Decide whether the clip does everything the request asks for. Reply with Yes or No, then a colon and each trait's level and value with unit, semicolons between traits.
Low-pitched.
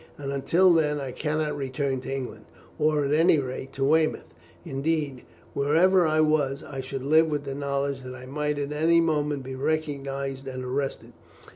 No: medium, 145 Hz